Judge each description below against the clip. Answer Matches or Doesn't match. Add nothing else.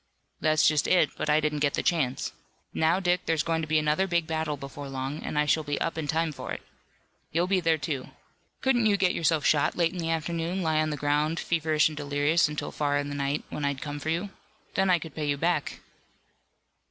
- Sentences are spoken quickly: Matches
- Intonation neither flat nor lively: Doesn't match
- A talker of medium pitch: Matches